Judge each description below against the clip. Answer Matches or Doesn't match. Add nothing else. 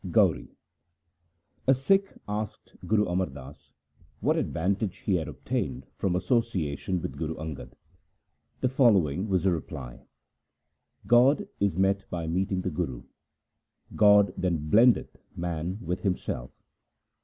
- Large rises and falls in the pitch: Doesn't match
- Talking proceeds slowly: Matches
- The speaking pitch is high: Doesn't match